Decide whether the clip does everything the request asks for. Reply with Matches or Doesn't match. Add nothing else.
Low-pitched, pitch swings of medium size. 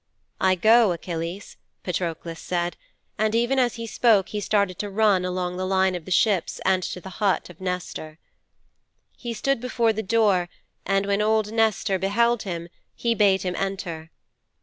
Doesn't match